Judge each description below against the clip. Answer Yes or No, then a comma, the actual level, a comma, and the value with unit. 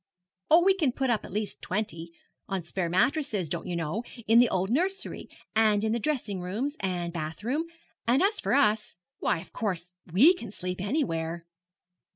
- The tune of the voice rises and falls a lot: Yes, wide, 6.9 semitones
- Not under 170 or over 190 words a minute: Yes, average, 185 wpm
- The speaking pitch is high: Yes, high, 210 Hz